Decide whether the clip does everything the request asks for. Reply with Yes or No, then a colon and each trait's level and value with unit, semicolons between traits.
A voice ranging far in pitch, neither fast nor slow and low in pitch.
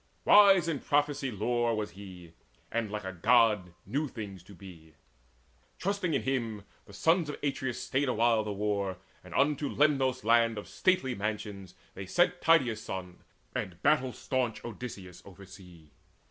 Yes: wide, 5.7 semitones; average, 150 wpm; low, 115 Hz